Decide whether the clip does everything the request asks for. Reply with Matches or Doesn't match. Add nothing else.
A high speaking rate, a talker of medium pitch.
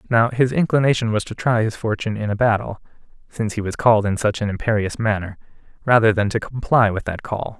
Doesn't match